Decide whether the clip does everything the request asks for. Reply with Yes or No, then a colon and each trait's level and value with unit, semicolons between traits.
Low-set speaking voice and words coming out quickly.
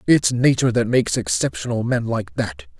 No: low, 110 Hz; average, 170 wpm